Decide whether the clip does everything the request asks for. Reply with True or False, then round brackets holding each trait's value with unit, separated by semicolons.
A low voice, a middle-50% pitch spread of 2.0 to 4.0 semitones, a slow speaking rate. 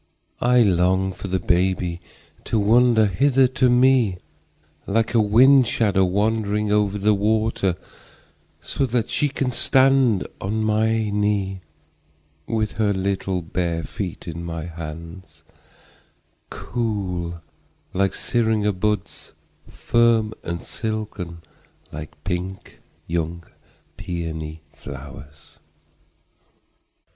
False (100 Hz; 4.4 semitones; 90 wpm)